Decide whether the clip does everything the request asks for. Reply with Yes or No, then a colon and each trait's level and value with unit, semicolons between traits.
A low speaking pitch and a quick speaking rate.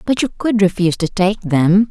No: high, 195 Hz; fast, 220 wpm